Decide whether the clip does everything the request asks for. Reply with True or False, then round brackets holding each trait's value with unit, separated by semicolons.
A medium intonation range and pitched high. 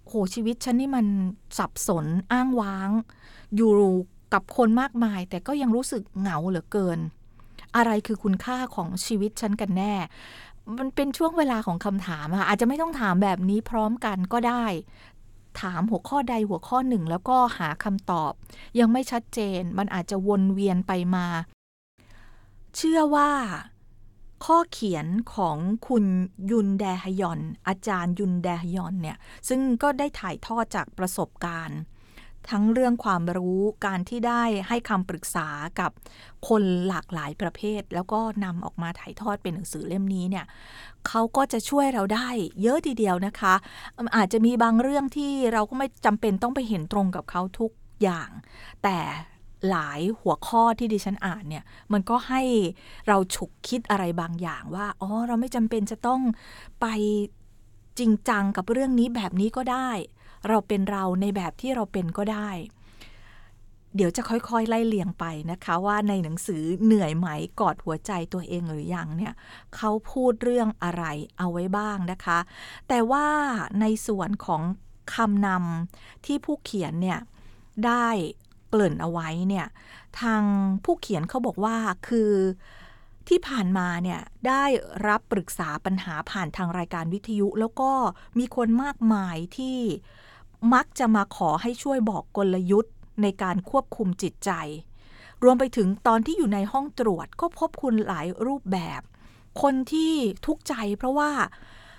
True (4.8 semitones; 205 Hz)